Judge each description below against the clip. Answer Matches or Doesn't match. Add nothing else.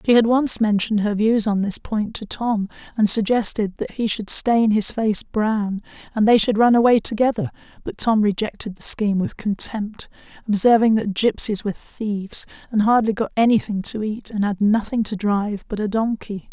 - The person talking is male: Doesn't match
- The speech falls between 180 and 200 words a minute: Matches